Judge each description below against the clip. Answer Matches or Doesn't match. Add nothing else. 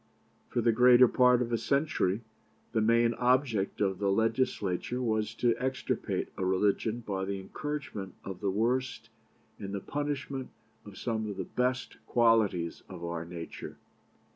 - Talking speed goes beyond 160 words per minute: Doesn't match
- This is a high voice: Doesn't match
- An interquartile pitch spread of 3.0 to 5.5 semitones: Matches